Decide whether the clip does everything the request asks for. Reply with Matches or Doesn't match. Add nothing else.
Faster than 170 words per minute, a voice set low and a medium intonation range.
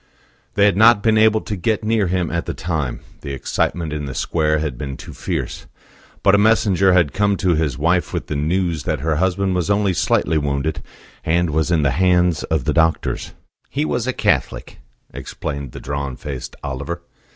Matches